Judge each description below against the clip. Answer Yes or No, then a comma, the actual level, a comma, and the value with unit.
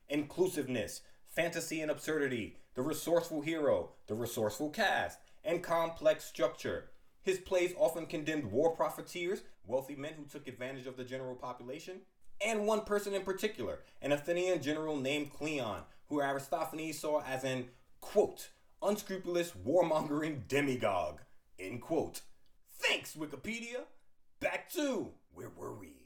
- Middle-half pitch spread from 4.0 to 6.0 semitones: Yes, average, 4.4 semitones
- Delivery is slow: Yes, slow, 130 wpm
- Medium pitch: Yes, medium, 155 Hz